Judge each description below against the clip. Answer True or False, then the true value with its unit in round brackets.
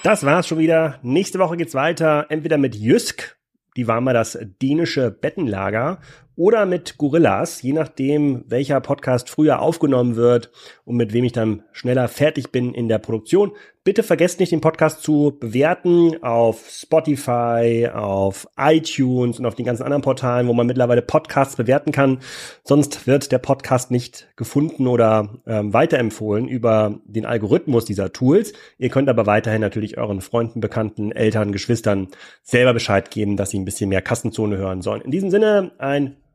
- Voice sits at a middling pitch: False (125 Hz)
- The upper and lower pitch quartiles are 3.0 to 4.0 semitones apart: False (4.8 semitones)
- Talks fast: False (165 wpm)